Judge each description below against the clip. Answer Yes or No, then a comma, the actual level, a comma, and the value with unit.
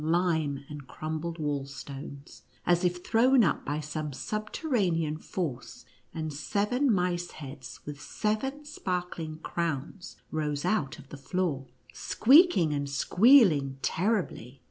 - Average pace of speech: No, slow, 120 wpm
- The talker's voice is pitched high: No, medium, 165 Hz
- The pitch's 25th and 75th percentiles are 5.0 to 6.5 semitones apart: Yes, wide, 5.4 semitones